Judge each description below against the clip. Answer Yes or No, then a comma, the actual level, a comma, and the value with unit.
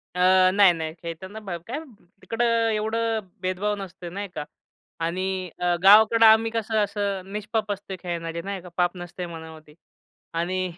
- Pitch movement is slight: No, average, 3.3 semitones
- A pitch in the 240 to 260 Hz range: No, high, 190 Hz